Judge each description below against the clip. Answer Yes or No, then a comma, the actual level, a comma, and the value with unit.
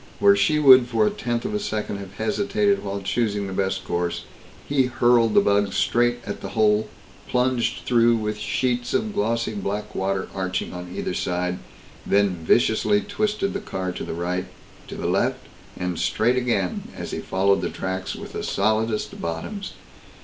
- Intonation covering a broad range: No, average, 4.8 semitones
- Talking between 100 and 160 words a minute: No, average, 175 wpm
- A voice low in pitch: Yes, low, 110 Hz